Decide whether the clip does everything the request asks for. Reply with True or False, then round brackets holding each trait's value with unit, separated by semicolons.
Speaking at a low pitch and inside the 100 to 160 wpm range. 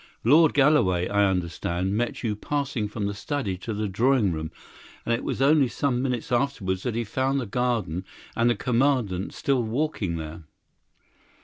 False (115 Hz; 170 wpm)